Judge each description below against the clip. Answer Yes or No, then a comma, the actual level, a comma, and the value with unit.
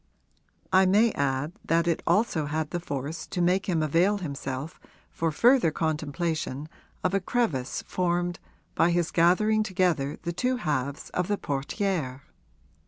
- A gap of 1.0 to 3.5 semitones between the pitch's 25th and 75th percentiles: No, average, 4.1 semitones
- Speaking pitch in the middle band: Yes, medium, 170 Hz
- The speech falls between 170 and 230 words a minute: No, average, 145 wpm